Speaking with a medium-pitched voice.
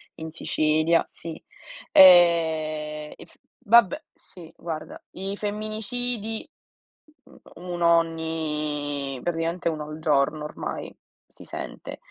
Yes: medium, 165 Hz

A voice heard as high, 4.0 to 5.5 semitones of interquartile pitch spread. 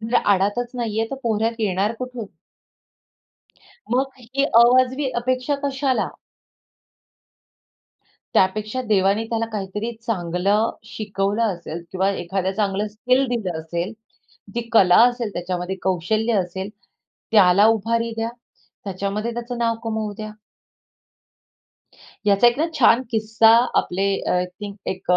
No: high, 215 Hz; average, 3.4 semitones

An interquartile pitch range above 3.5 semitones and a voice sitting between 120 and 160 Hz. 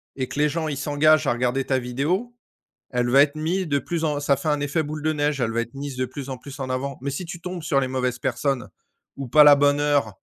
No: average, 2.8 semitones; medium, 140 Hz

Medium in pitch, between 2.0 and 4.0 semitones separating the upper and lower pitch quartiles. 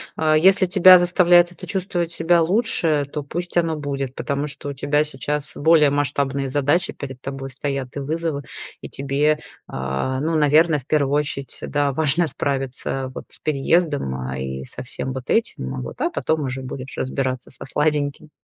Yes: medium, 145 Hz; average, 3.1 semitones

